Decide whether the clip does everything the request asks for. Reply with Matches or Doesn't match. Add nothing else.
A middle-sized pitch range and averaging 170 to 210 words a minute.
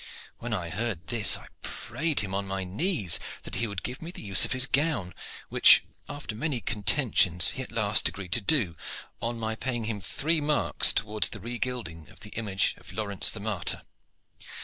Matches